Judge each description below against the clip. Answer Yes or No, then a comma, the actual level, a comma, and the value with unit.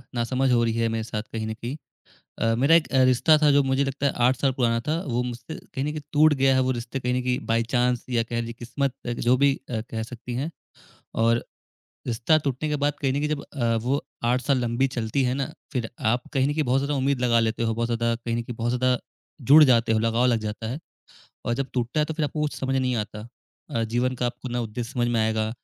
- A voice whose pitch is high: No, low, 125 Hz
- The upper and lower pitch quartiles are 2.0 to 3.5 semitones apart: Yes, average, 2.7 semitones